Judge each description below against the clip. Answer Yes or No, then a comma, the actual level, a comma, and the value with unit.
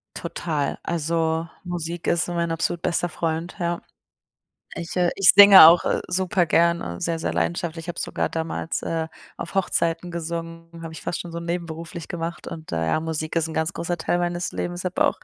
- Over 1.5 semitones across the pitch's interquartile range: No, narrow, 1.2 semitones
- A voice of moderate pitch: Yes, medium, 170 Hz